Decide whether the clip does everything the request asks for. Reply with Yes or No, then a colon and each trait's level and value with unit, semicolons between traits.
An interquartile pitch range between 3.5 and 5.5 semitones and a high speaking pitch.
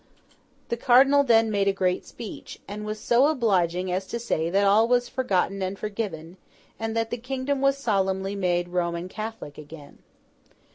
Yes: average, 4.4 semitones; high, 205 Hz